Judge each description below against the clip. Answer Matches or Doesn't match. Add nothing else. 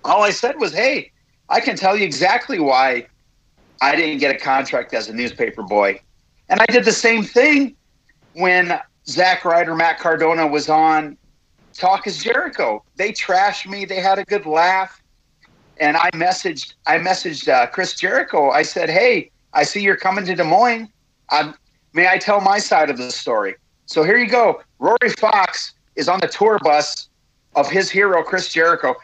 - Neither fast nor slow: Matches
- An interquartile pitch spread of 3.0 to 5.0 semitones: Doesn't match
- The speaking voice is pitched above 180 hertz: Matches